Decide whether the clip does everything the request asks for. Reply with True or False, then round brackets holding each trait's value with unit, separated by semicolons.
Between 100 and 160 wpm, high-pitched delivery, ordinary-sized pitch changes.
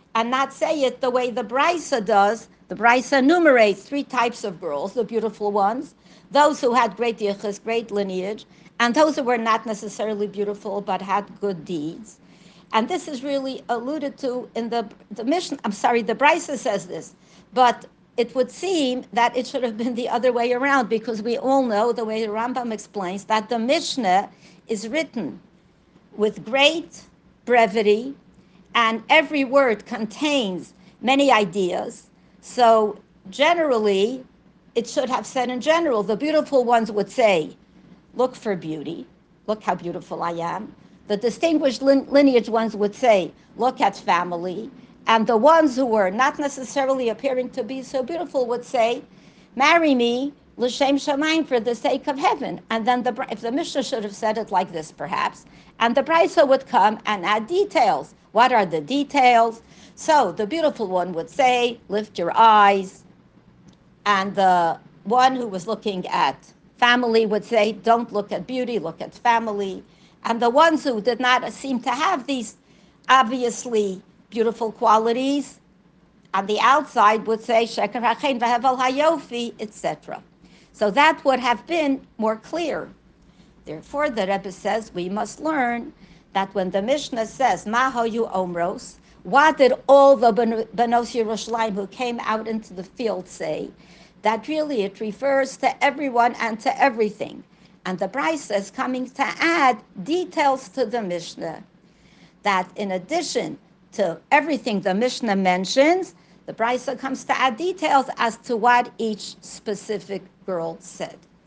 True (155 wpm; 235 Hz; 4.5 semitones)